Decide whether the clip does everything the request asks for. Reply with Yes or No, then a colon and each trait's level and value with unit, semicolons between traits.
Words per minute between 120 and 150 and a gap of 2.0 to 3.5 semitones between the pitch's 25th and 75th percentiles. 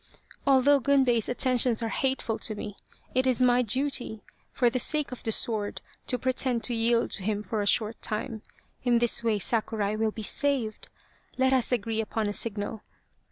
No: average, 185 wpm; average, 2.9 semitones